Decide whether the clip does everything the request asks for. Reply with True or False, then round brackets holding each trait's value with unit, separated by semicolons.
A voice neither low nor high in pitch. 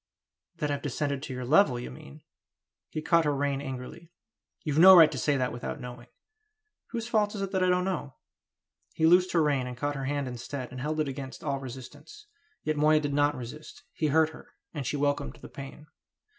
True (145 Hz)